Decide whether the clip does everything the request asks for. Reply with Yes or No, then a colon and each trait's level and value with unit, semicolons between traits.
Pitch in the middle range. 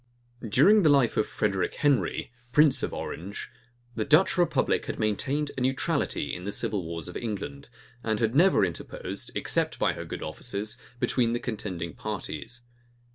No: low, 115 Hz